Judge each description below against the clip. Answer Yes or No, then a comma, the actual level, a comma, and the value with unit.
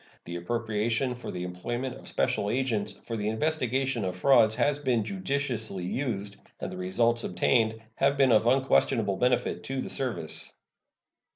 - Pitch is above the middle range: No, low, 115 Hz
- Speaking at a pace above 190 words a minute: No, average, 155 wpm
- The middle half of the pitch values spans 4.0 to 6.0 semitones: Yes, average, 4.4 semitones